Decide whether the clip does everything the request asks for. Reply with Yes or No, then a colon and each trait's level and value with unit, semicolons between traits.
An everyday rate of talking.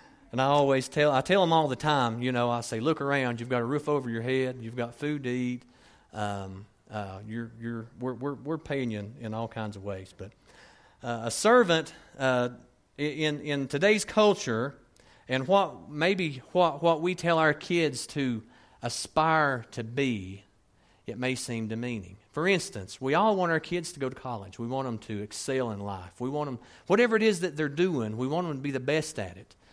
No: fast, 210 wpm